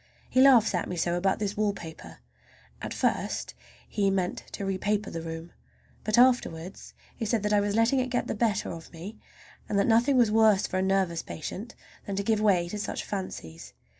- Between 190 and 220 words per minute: Yes, average, 195 wpm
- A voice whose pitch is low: No, high, 200 Hz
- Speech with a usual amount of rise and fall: Yes, average, 3.5 semitones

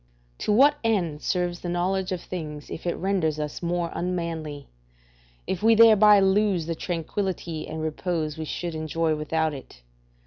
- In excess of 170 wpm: No, average, 160 wpm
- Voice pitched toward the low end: No, medium, 175 Hz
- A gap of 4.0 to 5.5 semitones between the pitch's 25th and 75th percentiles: No, average, 3.3 semitones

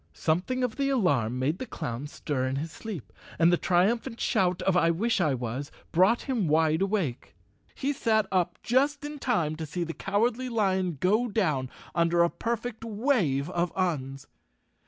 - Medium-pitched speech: Yes, medium, 180 Hz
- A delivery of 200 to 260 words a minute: No, average, 175 wpm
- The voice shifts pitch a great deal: Yes, wide, 6.7 semitones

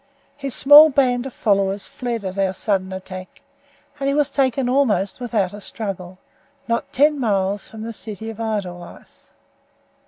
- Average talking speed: Yes, average, 155 wpm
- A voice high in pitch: Yes, high, 220 Hz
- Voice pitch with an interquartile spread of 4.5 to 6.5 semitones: Yes, average, 5.0 semitones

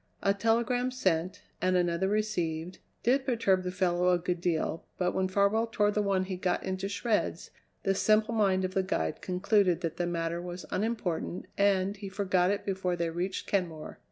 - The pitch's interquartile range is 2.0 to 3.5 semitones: Yes, narrow, 2.4 semitones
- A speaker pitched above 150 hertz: Yes, medium, 185 Hz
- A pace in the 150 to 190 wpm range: Yes, average, 185 wpm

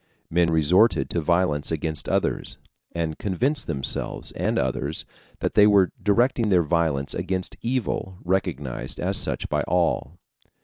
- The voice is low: Yes, very low, 85 Hz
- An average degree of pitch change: Yes, average, 4.2 semitones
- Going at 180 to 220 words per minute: No, slow, 135 wpm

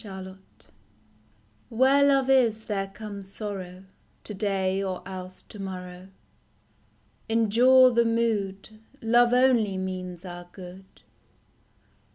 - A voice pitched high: Yes, high, 200 Hz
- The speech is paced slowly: Yes, slow, 100 wpm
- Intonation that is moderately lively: Yes, average, 3.5 semitones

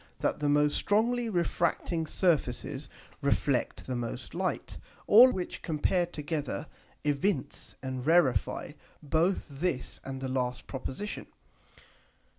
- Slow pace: Yes, slow, 110 wpm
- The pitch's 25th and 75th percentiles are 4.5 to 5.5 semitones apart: Yes, average, 4.8 semitones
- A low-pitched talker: No, medium, 150 Hz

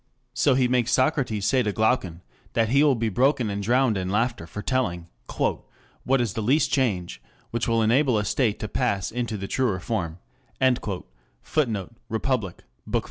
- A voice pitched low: Yes, low, 115 Hz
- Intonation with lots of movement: No, average, 4.0 semitones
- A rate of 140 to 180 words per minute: Yes, average, 170 wpm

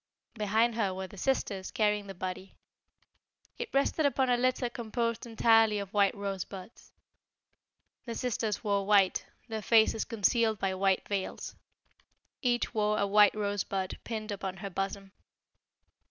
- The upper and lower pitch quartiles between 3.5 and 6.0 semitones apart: No, average, 2.8 semitones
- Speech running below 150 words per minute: Yes, average, 140 wpm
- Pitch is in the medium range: No, high, 210 Hz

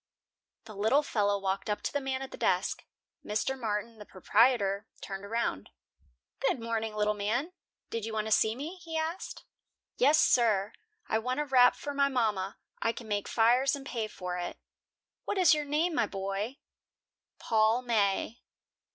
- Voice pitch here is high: Yes, high, 225 Hz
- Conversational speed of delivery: Yes, average, 170 wpm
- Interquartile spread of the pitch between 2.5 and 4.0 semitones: No, average, 4.4 semitones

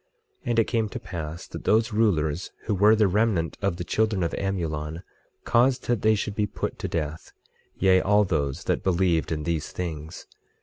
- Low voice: Yes, very low, 95 Hz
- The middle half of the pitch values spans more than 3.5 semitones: Yes, average, 4.6 semitones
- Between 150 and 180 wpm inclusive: No, average, 190 wpm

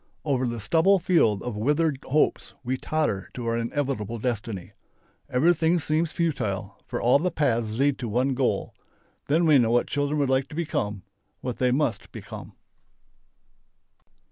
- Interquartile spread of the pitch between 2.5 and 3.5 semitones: No, average, 4.7 semitones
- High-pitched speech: No, low, 130 Hz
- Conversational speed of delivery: Yes, average, 150 wpm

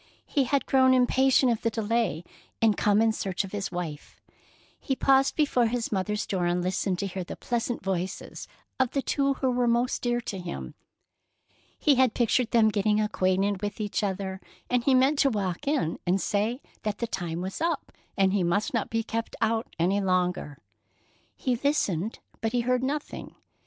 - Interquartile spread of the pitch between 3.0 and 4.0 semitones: No, average, 4.8 semitones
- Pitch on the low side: No, high, 220 Hz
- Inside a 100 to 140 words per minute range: No, average, 185 wpm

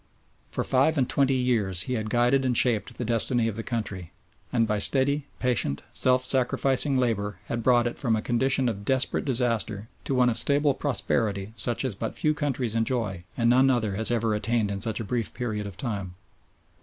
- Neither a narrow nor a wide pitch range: Yes, average, 3.2 semitones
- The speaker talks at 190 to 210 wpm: Yes, average, 195 wpm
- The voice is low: Yes, low, 120 Hz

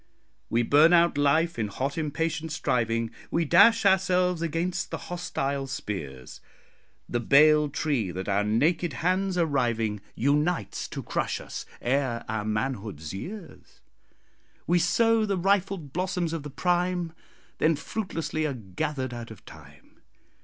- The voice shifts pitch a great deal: Yes, wide, 7.0 semitones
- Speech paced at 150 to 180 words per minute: No, average, 140 wpm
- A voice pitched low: No, medium, 150 Hz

